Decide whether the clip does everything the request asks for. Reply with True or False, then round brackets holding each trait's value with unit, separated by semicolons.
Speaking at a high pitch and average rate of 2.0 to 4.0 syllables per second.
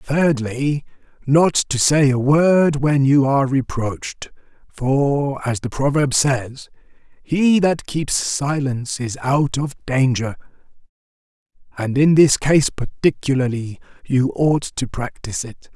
False (135 Hz; 3.7 syllables/s)